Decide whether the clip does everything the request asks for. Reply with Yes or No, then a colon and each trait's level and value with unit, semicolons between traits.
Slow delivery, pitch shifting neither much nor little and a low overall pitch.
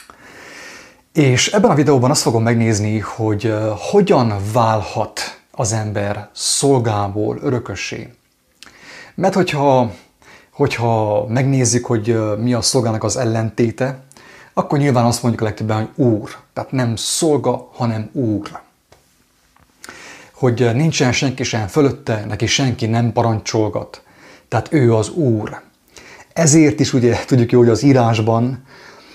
Yes: slow, 120 wpm; average, 3.5 semitones; low, 120 Hz